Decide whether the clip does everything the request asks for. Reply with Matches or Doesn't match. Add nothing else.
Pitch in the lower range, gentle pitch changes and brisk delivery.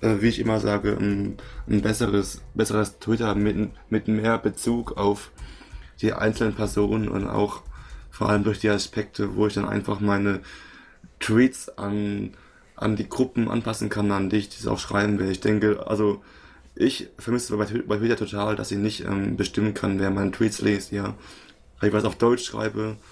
Doesn't match